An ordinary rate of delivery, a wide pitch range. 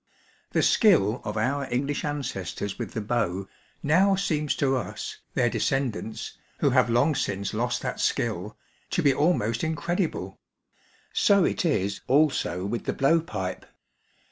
Yes: average, 145 wpm; wide, 6.5 semitones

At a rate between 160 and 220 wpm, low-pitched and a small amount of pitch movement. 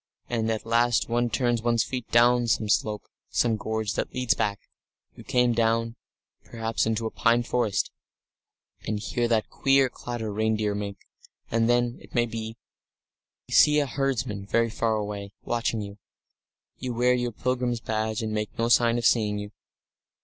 Yes: average, 165 wpm; low, 115 Hz; narrow, 1.8 semitones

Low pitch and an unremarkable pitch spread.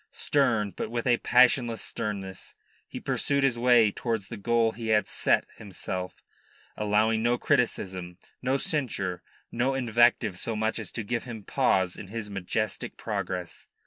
Yes: low, 110 Hz; average, 3.2 semitones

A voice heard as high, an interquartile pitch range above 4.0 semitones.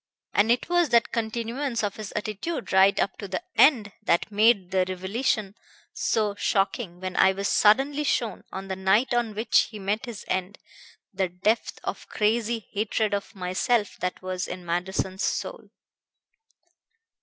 No: high, 205 Hz; average, 3.4 semitones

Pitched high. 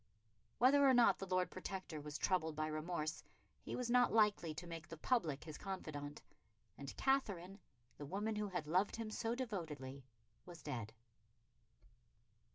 No: medium, 180 Hz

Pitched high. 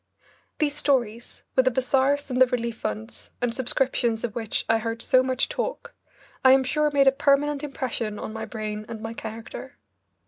Yes: very high, 250 Hz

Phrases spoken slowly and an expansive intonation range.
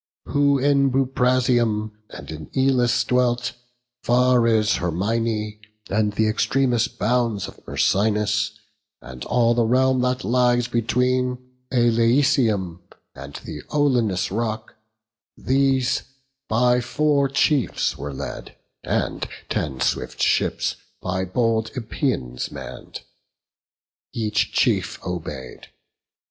No: slow, 105 wpm; average, 3.3 semitones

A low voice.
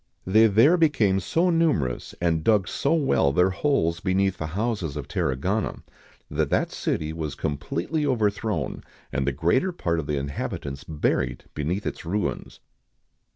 Yes: very low, 95 Hz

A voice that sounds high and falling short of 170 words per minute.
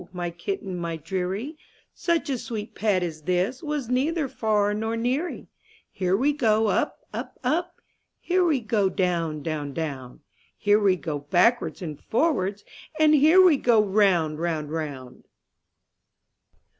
Yes: high, 205 Hz; average, 145 wpm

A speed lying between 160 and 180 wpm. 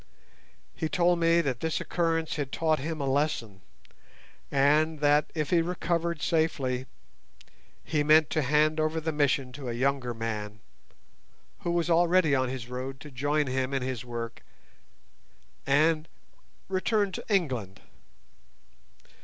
No: slow, 135 wpm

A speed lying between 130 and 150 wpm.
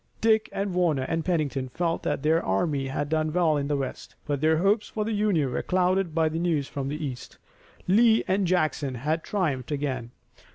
No: average, 200 wpm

